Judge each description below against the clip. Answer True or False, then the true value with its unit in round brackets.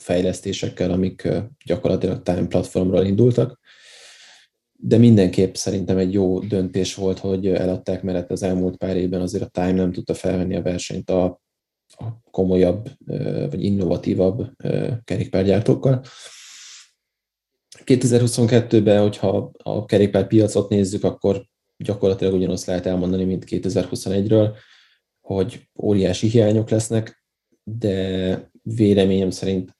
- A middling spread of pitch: True (3.0 semitones)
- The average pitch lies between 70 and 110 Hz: True (95 Hz)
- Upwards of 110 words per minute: False (105 wpm)